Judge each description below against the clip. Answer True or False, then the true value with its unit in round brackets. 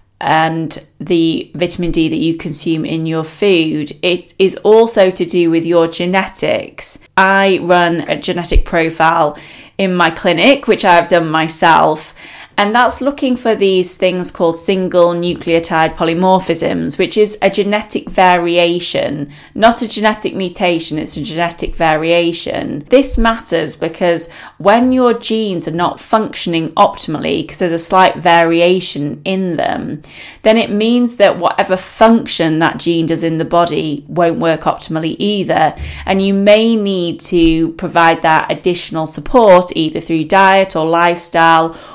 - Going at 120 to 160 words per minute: True (145 wpm)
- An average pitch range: True (3.0 semitones)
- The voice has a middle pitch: True (175 Hz)